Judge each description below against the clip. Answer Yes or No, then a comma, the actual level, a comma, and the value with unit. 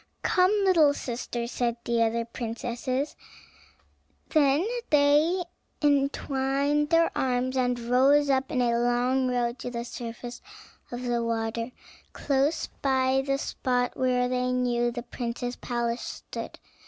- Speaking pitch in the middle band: No, very high, 250 Hz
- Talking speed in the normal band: No, slow, 130 wpm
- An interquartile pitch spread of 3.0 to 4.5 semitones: No, narrow, 2.6 semitones